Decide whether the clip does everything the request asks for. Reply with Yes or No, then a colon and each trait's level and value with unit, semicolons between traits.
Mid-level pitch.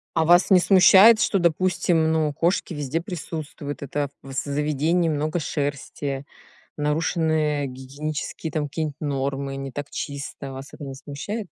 Yes: medium, 150 Hz